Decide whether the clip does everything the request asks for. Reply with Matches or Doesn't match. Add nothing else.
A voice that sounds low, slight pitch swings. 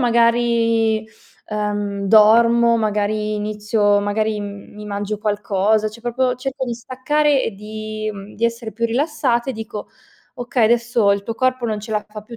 Doesn't match